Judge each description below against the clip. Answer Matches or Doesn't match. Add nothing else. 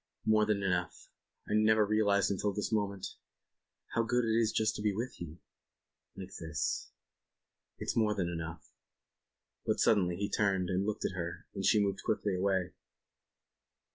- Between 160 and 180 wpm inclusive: Matches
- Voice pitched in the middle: Doesn't match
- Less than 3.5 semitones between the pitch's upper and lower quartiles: Matches